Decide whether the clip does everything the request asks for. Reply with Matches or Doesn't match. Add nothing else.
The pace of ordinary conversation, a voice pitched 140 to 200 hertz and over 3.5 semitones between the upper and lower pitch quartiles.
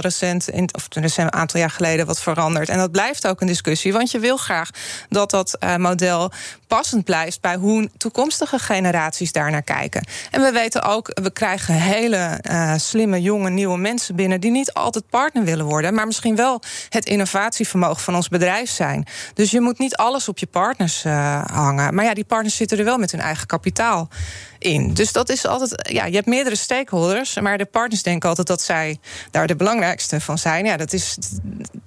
Matches